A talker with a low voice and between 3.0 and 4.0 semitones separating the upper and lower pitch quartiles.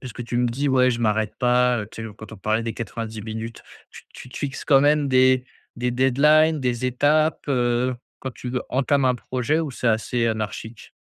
No: low, 125 Hz; narrow, 2.6 semitones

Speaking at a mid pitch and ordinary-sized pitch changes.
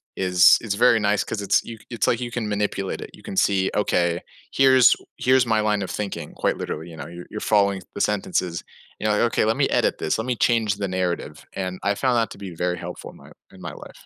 No: low, 100 Hz; average, 3.4 semitones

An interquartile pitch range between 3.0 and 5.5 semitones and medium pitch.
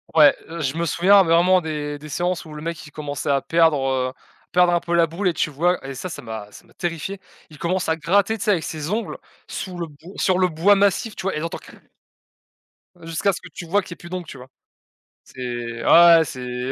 Yes: average, 3.7 semitones; medium, 165 Hz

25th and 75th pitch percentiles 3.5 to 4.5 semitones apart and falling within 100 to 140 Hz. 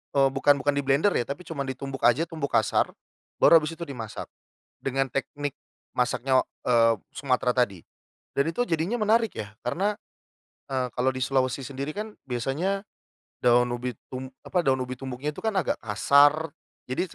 Yes: average, 3.9 semitones; low, 135 Hz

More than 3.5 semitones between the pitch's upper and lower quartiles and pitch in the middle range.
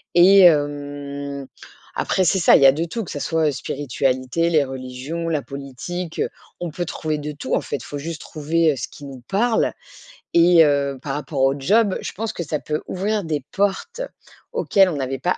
Yes: average, 3.9 semitones; medium, 150 Hz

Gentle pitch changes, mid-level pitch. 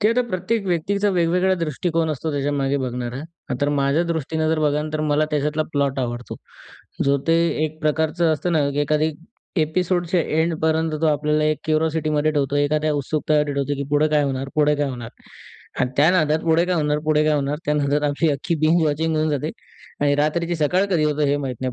Yes: narrow, 2.0 semitones; medium, 155 Hz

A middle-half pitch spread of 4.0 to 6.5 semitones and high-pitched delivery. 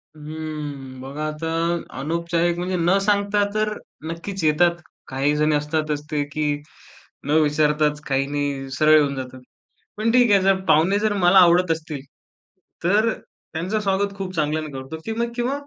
No: average, 4.5 semitones; medium, 160 Hz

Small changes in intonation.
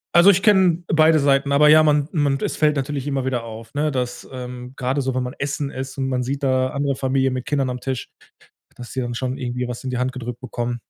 Yes: narrow, 2.3 semitones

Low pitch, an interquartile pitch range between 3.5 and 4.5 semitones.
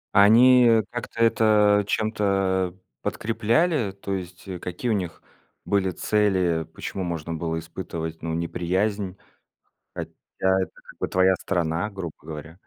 Yes: very low, 95 Hz; average, 3.8 semitones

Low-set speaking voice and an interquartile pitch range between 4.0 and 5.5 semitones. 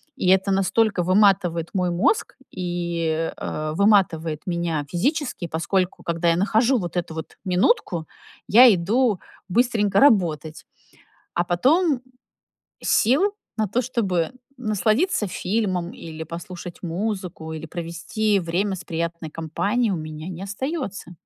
No: medium, 185 Hz; average, 4.3 semitones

